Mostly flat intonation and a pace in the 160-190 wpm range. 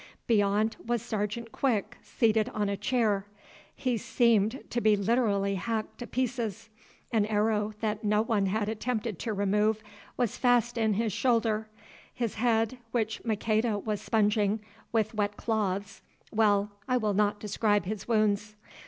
No: narrow, 1.9 semitones; average, 145 wpm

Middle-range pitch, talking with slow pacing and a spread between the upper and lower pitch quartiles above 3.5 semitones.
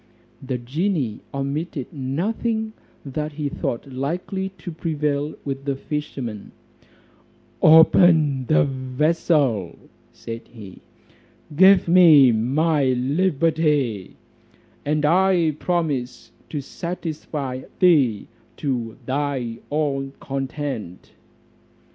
Yes: medium, 145 Hz; slow, 85 wpm; average, 3.9 semitones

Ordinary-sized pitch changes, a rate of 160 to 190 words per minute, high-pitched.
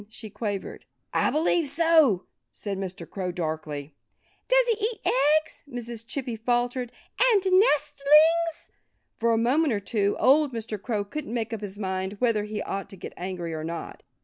No: wide, 7.2 semitones; average, 165 wpm; high, 235 Hz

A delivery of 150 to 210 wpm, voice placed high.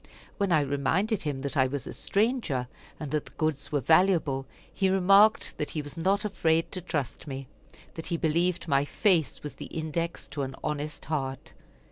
No: average, 185 wpm; medium, 155 Hz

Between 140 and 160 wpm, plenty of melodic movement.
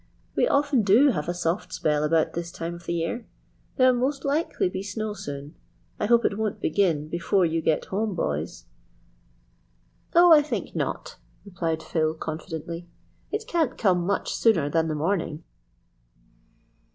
Yes: average, 155 wpm; wide, 5.9 semitones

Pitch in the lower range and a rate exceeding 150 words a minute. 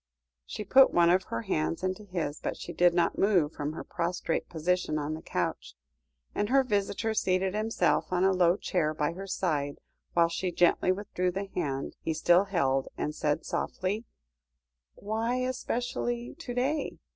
No: medium, 185 Hz; average, 170 wpm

